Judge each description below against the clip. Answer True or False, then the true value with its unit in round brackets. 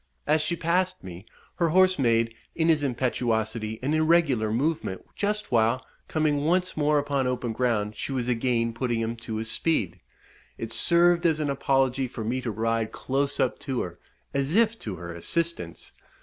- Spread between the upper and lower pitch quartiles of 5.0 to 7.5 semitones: True (5.6 semitones)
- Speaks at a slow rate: False (175 wpm)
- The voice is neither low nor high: False (130 Hz)